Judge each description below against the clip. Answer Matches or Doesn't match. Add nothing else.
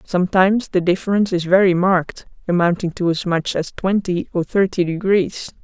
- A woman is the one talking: Matches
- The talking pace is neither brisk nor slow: Matches